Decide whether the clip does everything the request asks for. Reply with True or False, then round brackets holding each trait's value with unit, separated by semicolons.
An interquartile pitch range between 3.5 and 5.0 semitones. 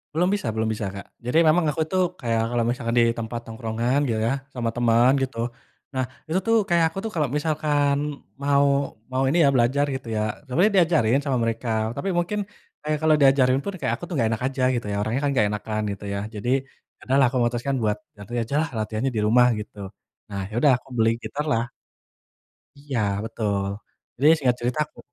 True (4.2 semitones)